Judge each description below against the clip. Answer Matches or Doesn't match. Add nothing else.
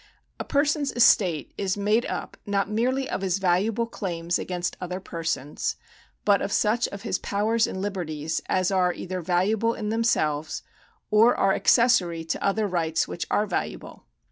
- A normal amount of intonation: Matches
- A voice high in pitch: Matches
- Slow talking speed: Doesn't match